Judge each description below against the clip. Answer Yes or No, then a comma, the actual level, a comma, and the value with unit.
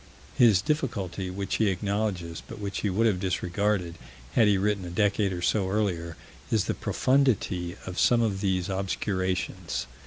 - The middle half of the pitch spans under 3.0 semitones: Yes, narrow, 2.6 semitones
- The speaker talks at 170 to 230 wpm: No, average, 160 wpm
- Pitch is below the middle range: Yes, very low, 95 Hz